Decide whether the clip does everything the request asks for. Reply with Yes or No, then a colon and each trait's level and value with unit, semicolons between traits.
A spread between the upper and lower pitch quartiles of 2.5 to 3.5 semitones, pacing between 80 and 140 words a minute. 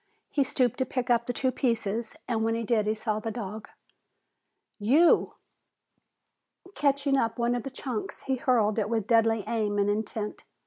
No: average, 2.8 semitones; average, 175 wpm